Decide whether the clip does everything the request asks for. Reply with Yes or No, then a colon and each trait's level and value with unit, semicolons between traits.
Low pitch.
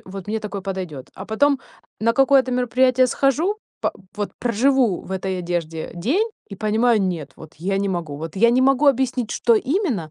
No: high, 220 Hz